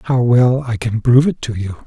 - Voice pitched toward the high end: No, low, 120 Hz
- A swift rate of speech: Yes, fast, 255 wpm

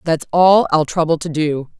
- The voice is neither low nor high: Yes, medium, 160 Hz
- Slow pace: No, average, 200 wpm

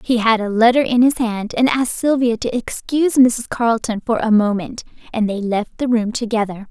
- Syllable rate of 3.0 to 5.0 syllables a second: No, 5.3 syllables/s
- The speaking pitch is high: Yes, high, 230 Hz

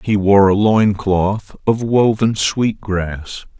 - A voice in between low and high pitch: No, low, 100 Hz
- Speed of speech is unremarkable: Yes, average, 150 wpm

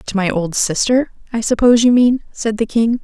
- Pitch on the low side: No, high, 225 Hz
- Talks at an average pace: No, fast, 215 wpm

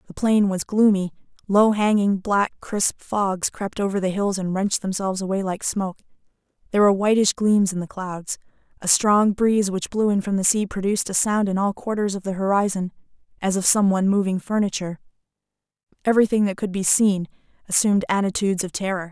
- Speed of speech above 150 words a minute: Yes, average, 185 wpm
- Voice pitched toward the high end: Yes, high, 195 Hz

